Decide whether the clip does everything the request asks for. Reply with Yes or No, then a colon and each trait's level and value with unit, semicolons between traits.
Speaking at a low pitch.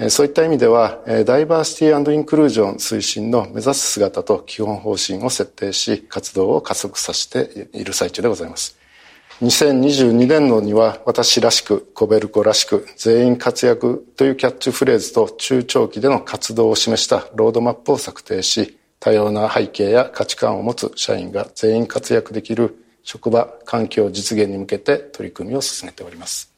Yes: low, 120 Hz